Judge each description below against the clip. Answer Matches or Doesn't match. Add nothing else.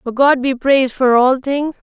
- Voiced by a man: Doesn't match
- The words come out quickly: Matches